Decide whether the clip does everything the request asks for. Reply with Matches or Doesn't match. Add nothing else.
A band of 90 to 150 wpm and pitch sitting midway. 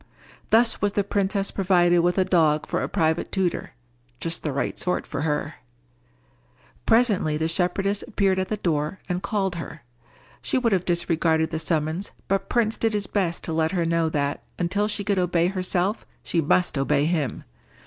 Doesn't match